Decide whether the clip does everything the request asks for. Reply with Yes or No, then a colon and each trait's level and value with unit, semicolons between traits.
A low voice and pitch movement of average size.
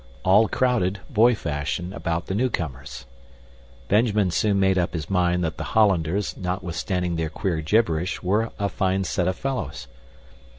Yes: very low, 95 Hz; average, 3.6 semitones